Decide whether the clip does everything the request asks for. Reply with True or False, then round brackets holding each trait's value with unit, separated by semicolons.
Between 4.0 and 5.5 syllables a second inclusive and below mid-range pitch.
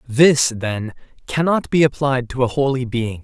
True (4.3 syllables/s; 130 Hz)